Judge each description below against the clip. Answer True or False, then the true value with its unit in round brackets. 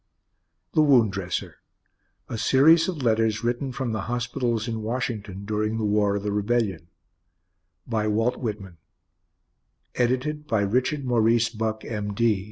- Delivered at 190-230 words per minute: False (140 wpm)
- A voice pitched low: True (115 Hz)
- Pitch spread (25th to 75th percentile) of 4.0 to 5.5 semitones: False (2.8 semitones)